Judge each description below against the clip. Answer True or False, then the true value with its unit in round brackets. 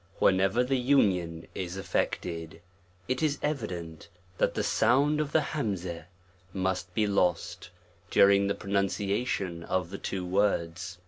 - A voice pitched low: True (95 Hz)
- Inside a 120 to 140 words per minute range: True (135 wpm)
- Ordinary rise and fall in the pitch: True (4.8 semitones)